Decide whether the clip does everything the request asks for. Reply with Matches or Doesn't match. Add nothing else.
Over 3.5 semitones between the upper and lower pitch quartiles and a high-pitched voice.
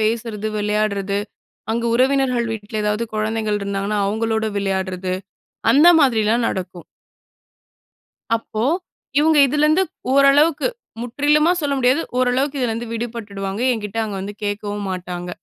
Matches